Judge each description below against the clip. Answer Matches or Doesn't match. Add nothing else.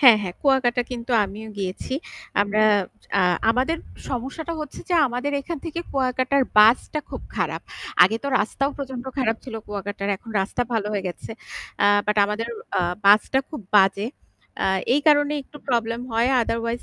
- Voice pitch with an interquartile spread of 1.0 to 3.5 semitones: Doesn't match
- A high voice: Matches